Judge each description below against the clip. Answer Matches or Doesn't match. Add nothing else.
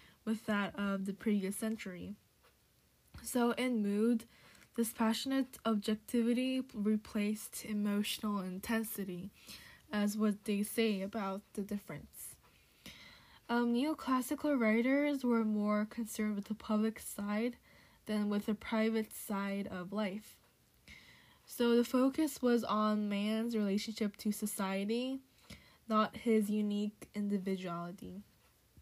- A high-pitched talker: Matches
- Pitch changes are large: Doesn't match